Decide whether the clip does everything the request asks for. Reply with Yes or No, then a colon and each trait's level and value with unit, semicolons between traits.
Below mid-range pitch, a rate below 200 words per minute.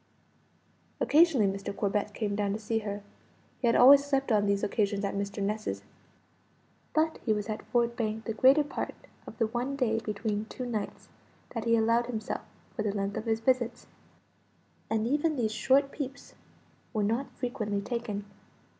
No: high, 225 Hz; average, 165 wpm